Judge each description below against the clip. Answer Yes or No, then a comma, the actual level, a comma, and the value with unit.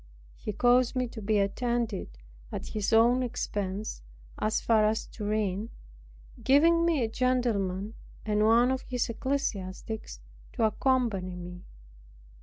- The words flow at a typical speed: No, slow, 125 wpm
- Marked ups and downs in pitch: No, average, 3.6 semitones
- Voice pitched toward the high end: Yes, high, 220 Hz